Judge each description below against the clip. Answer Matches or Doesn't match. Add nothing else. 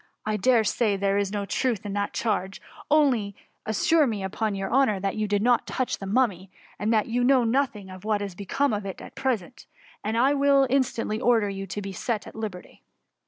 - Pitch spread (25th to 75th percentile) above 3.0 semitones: Matches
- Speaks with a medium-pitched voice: Doesn't match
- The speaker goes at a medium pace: Doesn't match